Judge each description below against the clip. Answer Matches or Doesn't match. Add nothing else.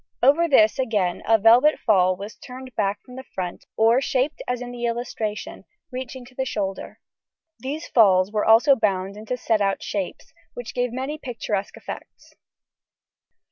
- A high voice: Matches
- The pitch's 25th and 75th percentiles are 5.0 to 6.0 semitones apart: Doesn't match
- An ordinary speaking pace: Matches